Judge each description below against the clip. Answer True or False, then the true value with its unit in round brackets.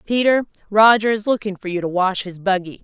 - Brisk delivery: True (210 wpm)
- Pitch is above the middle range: True (200 Hz)